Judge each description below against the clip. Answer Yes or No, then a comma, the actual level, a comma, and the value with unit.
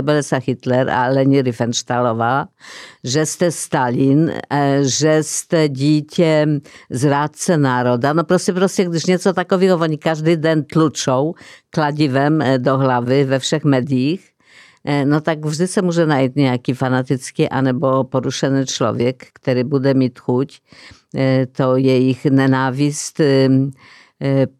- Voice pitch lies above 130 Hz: Yes, medium, 140 Hz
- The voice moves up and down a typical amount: Yes, average, 3.0 semitones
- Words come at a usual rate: No, slow, 110 wpm